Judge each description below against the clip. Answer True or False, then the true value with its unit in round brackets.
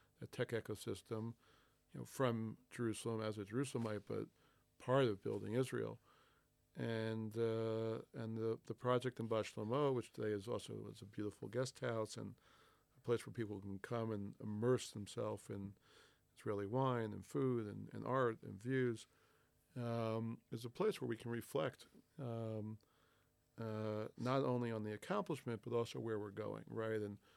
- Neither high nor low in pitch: False (115 Hz)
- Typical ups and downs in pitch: False (2.3 semitones)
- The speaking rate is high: False (160 wpm)